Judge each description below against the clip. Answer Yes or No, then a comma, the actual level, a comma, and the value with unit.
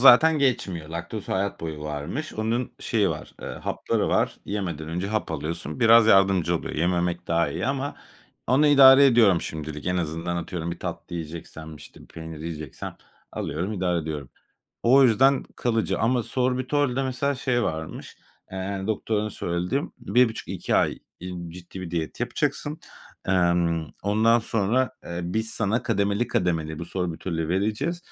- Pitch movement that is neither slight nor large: No, wide, 6.3 semitones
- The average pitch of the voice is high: No, very low, 95 Hz